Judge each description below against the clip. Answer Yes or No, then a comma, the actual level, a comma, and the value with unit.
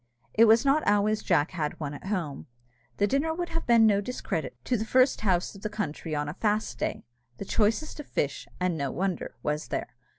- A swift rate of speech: Yes, fast, 210 wpm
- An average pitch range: No, wide, 6.1 semitones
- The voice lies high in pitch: Yes, high, 205 Hz